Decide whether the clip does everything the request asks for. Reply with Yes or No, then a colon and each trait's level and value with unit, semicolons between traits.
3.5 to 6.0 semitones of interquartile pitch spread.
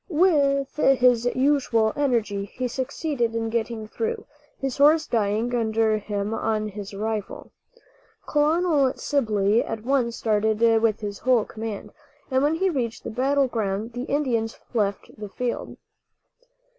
Yes: average, 4.2 semitones